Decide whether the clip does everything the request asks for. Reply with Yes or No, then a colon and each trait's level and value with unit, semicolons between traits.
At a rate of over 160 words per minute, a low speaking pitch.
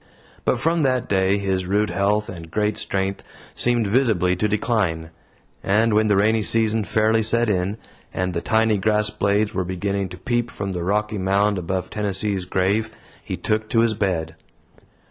Yes: average, 170 wpm; low, 105 Hz